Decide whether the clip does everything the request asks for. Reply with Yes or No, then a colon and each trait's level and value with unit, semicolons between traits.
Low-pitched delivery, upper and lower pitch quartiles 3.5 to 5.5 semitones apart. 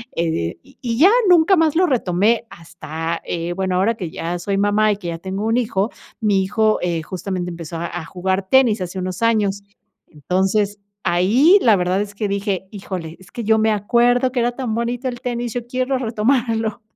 No: high, 205 Hz; average, 4.5 semitones